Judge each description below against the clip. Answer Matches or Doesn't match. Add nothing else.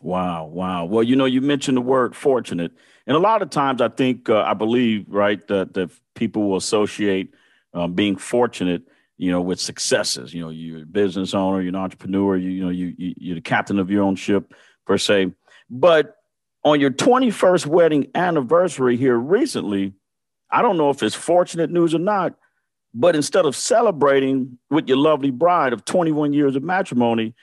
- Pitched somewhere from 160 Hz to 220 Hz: Doesn't match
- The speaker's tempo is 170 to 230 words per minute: Matches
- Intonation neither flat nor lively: Doesn't match